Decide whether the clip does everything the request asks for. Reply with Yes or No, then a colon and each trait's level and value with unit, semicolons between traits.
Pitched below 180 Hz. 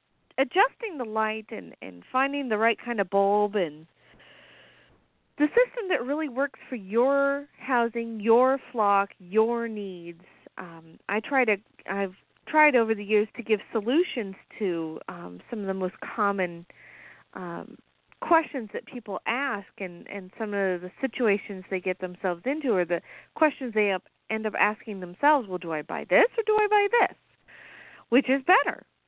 No: high, 220 Hz